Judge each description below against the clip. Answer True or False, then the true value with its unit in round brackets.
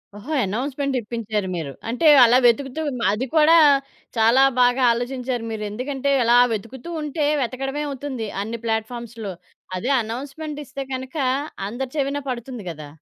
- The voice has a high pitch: True (250 Hz)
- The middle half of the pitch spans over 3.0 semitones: True (3.6 semitones)